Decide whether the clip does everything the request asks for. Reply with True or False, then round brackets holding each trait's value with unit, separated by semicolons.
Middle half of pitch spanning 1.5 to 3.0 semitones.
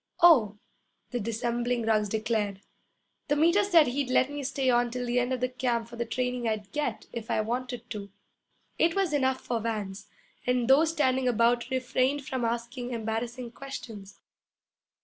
True (2.4 semitones)